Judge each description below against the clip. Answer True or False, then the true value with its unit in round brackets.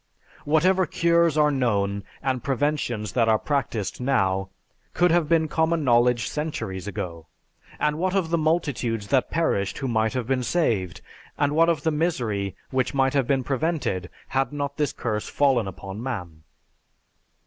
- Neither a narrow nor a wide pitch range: False (6.1 semitones)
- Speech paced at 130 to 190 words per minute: True (160 wpm)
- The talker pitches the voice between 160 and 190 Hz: False (135 Hz)